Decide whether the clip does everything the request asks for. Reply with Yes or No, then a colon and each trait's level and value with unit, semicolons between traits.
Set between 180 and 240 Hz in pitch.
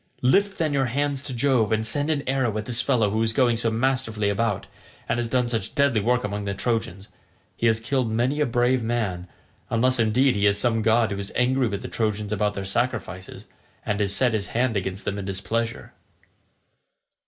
No: low, 115 Hz